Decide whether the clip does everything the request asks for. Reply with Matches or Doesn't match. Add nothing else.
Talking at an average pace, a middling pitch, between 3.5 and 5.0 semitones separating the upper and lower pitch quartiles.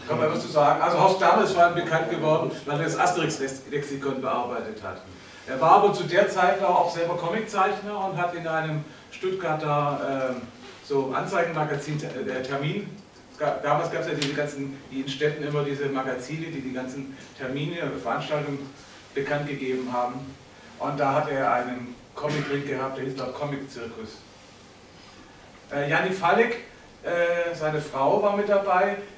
Matches